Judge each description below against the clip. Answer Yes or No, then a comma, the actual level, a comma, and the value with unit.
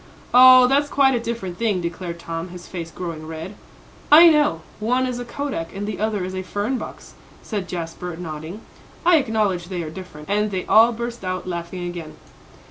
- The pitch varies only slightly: No, wide, 5.5 semitones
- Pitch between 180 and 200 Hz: Yes, high, 190 Hz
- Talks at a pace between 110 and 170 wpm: No, average, 190 wpm